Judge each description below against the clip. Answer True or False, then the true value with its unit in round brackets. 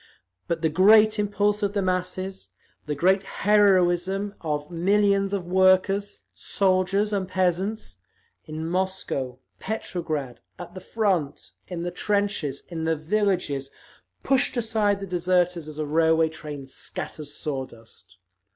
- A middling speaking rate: False (130 wpm)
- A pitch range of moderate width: True (4.1 semitones)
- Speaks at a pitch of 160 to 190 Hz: True (185 Hz)